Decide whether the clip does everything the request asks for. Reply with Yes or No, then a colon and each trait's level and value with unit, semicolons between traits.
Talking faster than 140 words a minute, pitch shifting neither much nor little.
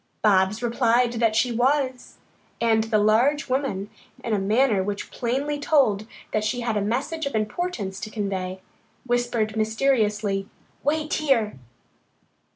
No: slow, 135 wpm; average, 3.8 semitones